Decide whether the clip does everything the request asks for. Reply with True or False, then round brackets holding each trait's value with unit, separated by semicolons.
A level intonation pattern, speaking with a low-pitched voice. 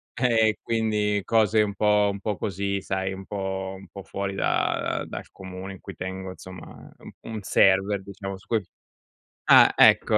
True (1.7 semitones; 100 Hz)